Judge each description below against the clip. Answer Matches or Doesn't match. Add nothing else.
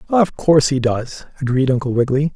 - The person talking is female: Doesn't match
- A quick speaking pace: Doesn't match